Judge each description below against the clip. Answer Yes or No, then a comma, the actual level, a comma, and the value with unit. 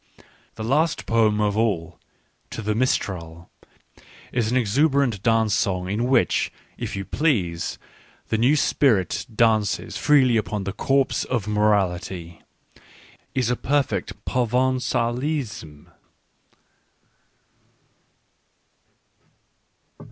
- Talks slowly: Yes, slow, 100 wpm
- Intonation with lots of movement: No, average, 4.6 semitones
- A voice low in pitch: Yes, low, 110 Hz